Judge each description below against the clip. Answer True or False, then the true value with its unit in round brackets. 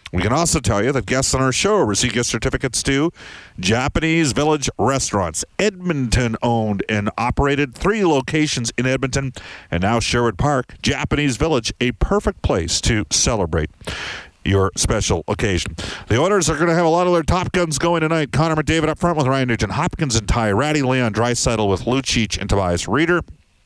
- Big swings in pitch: True (6.5 semitones)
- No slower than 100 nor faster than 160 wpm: False (180 wpm)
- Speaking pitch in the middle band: False (125 Hz)